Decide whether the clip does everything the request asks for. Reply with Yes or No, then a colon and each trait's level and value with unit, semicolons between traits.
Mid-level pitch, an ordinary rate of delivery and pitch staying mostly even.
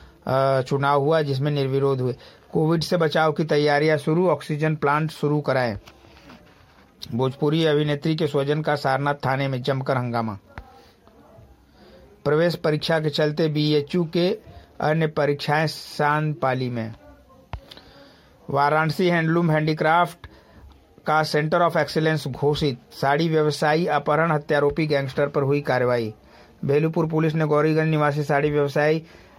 Yes: medium, 150 Hz; average, 120 wpm; narrow, 2.3 semitones